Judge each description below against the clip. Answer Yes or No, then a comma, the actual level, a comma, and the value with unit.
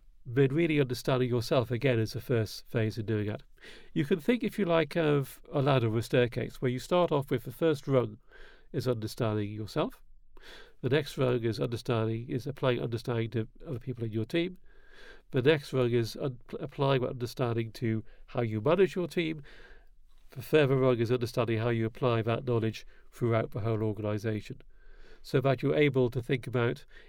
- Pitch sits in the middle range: No, low, 125 Hz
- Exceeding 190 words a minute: No, average, 185 wpm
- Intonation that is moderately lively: Yes, average, 3.7 semitones